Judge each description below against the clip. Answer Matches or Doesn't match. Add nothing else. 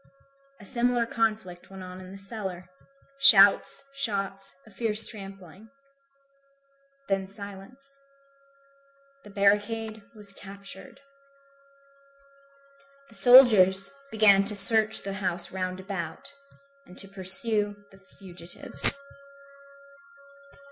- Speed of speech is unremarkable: Doesn't match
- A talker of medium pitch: Doesn't match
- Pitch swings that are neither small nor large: Doesn't match